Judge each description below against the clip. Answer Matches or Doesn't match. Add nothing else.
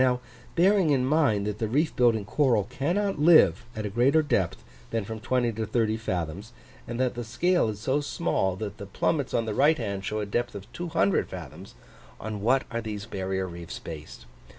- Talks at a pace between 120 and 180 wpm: Doesn't match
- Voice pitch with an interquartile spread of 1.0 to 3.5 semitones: Doesn't match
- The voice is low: Matches